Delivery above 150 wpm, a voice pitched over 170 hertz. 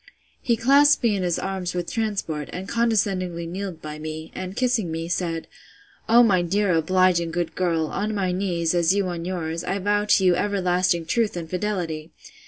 Yes: average, 185 wpm; medium, 185 Hz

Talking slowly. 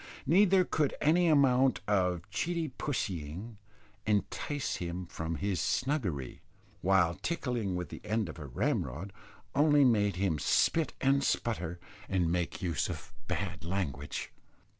Yes: slow, 130 wpm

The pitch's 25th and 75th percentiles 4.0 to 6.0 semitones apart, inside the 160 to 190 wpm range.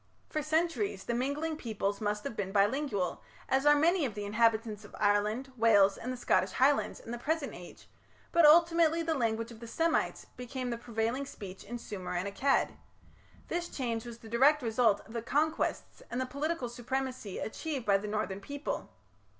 Yes: average, 5.3 semitones; average, 180 wpm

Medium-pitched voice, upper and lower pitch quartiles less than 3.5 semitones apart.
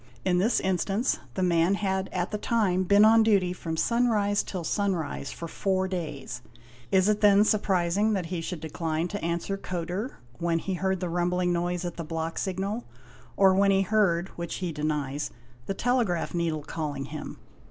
Yes: medium, 180 Hz; average, 3.0 semitones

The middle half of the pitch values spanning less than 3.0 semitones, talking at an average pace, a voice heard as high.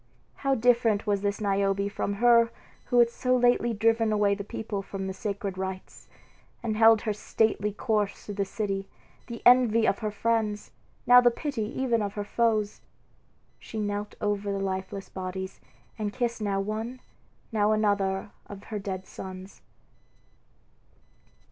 Yes: narrow, 2.4 semitones; average, 155 wpm; high, 210 Hz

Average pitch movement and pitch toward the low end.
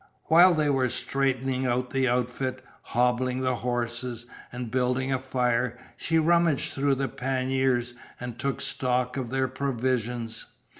No: narrow, 1.5 semitones; low, 130 Hz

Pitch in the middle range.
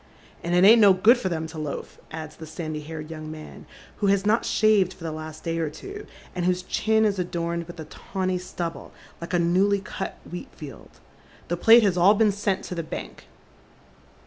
Yes: medium, 175 Hz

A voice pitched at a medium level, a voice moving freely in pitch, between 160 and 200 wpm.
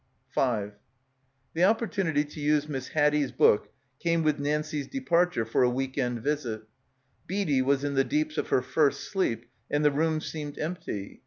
No: medium, 150 Hz; average, 3.7 semitones; average, 165 wpm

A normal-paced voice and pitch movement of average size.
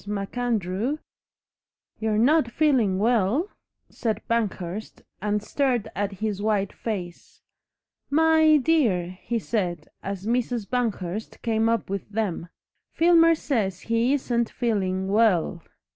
No: slow, 115 wpm; average, 4.1 semitones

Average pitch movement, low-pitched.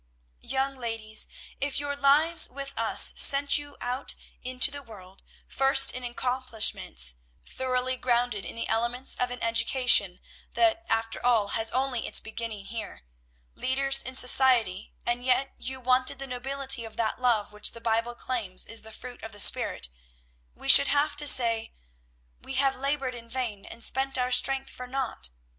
No: average, 3.0 semitones; very high, 250 Hz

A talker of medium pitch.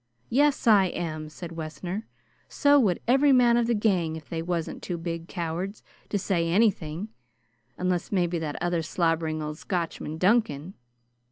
Yes: medium, 175 Hz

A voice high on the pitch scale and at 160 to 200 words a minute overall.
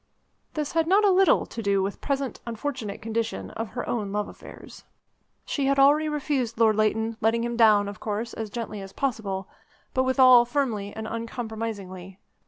Yes: high, 230 Hz; average, 180 wpm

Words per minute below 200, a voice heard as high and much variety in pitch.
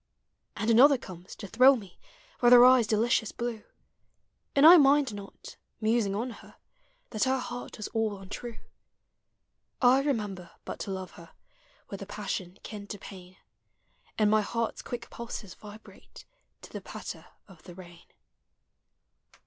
No: average, 150 wpm; high, 215 Hz; average, 3.6 semitones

